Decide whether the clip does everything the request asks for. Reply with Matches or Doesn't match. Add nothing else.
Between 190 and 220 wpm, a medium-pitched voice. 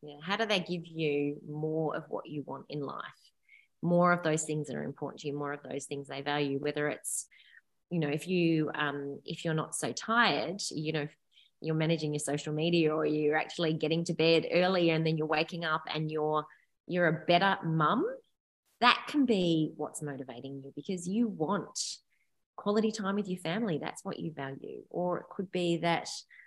Matches